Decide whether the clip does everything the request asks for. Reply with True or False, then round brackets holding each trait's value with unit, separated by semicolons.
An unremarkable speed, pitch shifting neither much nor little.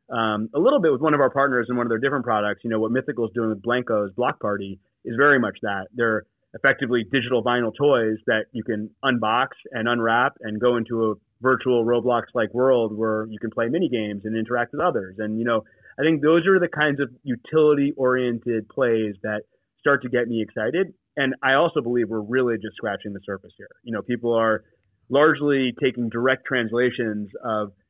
False (210 wpm; 3.1 semitones)